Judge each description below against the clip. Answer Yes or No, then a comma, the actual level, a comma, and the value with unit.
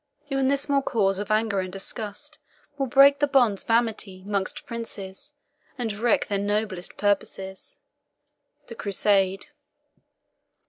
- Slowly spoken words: Yes, slow, 130 wpm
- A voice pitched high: Yes, high, 210 Hz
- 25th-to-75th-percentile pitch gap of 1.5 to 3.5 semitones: No, average, 4.1 semitones